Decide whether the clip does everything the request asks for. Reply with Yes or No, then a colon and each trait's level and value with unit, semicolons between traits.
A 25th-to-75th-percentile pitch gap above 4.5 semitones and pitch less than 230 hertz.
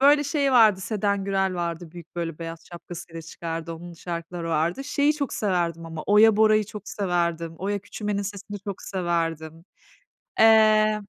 No: average, 4.1 semitones; medium, 185 Hz